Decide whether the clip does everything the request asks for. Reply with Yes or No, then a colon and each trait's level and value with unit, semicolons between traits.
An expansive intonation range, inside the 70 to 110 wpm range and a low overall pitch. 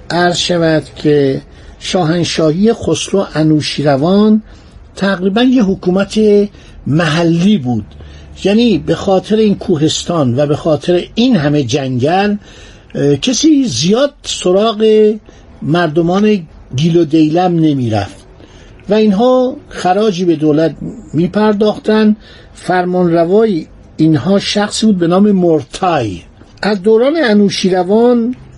No: wide, 5.8 semitones; slow, 105 wpm; medium, 180 Hz